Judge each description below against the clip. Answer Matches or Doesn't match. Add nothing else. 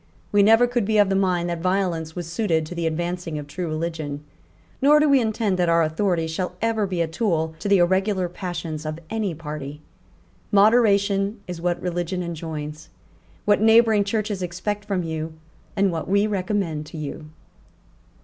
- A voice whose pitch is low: Doesn't match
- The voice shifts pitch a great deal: Doesn't match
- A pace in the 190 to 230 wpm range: Doesn't match